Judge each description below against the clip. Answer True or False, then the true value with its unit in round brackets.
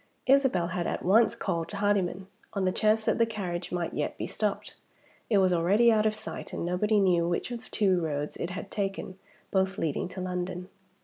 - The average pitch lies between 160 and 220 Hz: True (190 Hz)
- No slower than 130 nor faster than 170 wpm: False (195 wpm)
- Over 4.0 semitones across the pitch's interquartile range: False (3.3 semitones)